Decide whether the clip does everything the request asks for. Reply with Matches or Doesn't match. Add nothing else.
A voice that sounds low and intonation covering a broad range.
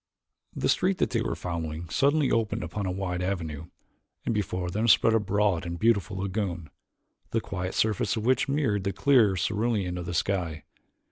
Doesn't match